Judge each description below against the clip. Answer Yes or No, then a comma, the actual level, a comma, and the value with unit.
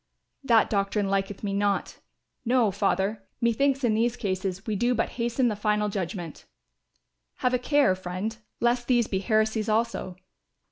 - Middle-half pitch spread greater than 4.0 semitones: No, average, 3.3 semitones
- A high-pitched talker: Yes, high, 215 Hz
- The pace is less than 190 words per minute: Yes, average, 150 wpm